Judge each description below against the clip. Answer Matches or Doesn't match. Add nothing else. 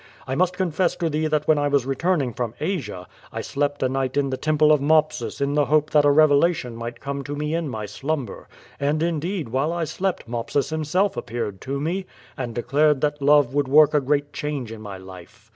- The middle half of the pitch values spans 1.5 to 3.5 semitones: Matches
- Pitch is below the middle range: Doesn't match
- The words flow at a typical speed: Doesn't match